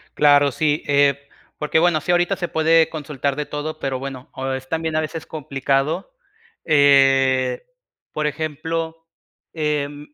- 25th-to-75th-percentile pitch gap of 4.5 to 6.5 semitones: No, narrow, 2.6 semitones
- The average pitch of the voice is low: No, medium, 150 Hz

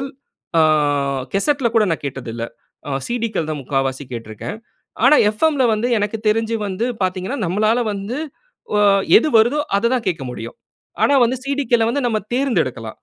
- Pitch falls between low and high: No, high, 215 Hz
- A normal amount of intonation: No, wide, 7.6 semitones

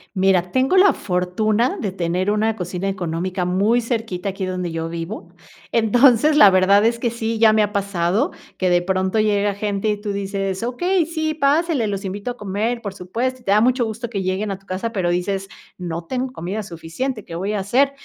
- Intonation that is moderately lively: Yes, average, 3.9 semitones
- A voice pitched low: No, high, 205 Hz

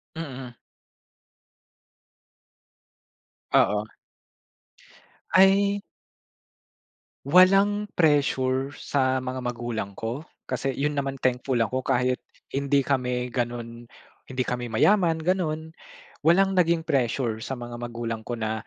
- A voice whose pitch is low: Yes, low, 130 Hz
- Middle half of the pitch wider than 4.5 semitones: Yes, average, 4.9 semitones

